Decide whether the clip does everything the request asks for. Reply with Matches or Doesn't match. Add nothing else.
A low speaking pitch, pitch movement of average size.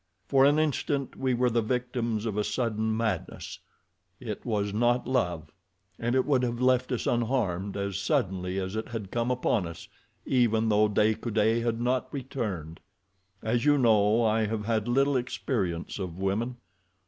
Matches